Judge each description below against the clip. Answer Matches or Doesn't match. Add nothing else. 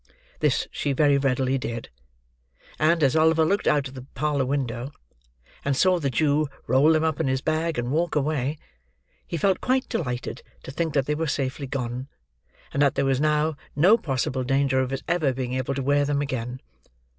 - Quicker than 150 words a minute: Matches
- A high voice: Doesn't match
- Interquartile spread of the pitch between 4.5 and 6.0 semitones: Doesn't match